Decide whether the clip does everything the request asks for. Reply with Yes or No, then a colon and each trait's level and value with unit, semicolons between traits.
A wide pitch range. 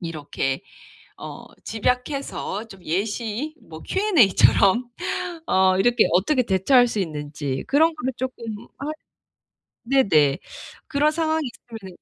Yes: wide, 6.7 semitones